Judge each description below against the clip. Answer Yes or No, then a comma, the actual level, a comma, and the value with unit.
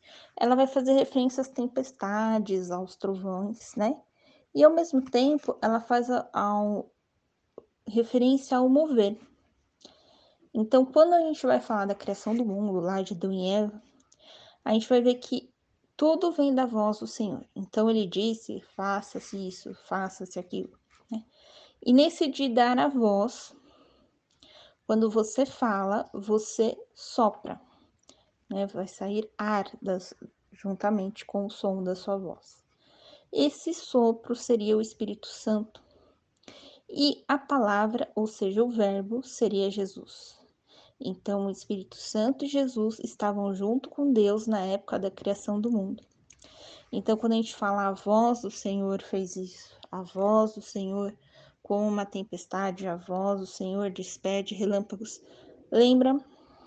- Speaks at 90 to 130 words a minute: No, average, 140 wpm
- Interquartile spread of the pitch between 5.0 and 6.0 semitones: No, average, 4.2 semitones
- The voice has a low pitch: No, high, 215 Hz